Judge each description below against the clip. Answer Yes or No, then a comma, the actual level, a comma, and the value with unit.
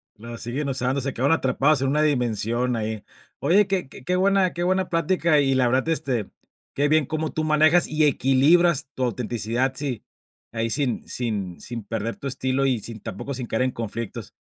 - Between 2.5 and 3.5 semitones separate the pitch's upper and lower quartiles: No, average, 4.6 semitones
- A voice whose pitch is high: No, low, 130 Hz